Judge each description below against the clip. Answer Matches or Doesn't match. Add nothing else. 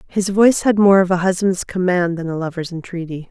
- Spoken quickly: Matches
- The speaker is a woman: Matches